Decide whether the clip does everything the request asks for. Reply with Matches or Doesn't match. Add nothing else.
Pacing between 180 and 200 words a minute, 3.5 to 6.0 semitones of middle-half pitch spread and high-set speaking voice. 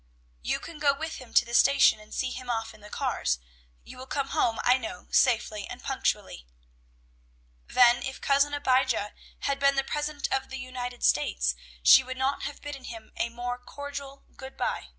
Doesn't match